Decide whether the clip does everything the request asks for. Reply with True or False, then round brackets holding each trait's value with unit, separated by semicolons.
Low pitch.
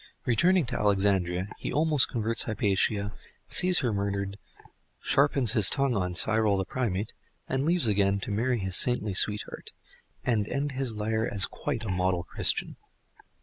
True (105 Hz)